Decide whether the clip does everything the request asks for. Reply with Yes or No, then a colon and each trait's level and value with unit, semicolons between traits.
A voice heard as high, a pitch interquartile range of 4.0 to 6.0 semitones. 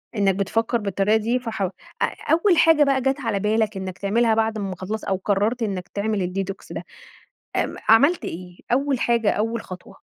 No: high, 220 Hz; average, 3.3 semitones